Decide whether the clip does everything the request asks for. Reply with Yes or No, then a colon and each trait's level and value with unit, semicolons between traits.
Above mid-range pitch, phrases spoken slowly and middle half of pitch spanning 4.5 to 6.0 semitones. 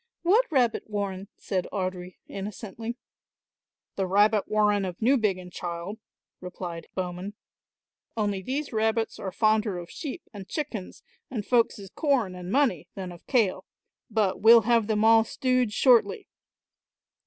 No: high, 210 Hz; slow, 130 wpm; average, 3.8 semitones